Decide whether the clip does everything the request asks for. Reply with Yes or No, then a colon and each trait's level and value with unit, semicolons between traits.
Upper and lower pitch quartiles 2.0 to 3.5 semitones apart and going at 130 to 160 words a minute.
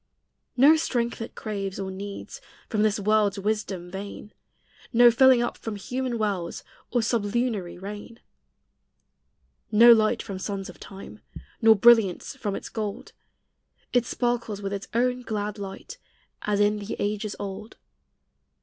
Yes: average, 2.9 semitones; average, 140 wpm